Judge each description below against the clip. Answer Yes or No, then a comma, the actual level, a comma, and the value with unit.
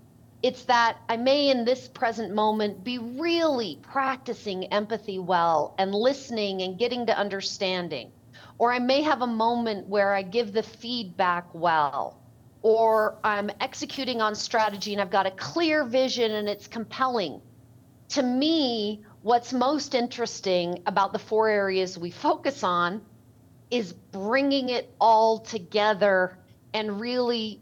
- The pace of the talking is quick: No, average, 140 wpm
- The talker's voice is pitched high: Yes, high, 220 Hz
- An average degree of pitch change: Yes, average, 3.9 semitones